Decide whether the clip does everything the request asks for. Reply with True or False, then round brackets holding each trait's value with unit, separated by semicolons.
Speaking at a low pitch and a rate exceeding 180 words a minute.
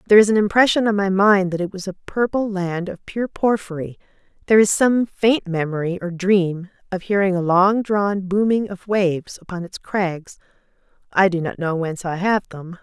False (190 Hz; 195 wpm)